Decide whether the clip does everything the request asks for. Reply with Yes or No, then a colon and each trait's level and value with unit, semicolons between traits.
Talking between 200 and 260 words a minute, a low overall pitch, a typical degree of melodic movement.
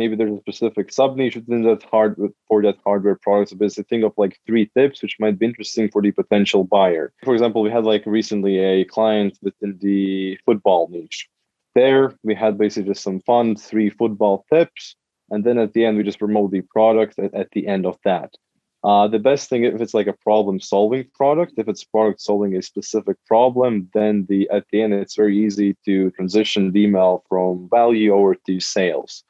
No: fast, 205 wpm; low, 105 Hz; narrow, 2.1 semitones